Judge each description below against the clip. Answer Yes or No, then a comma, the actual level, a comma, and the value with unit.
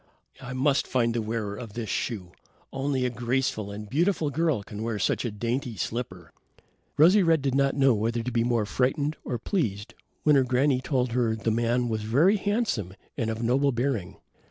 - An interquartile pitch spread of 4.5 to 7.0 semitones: No, average, 3.7 semitones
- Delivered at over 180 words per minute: Yes, average, 190 wpm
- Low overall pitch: Yes, low, 125 Hz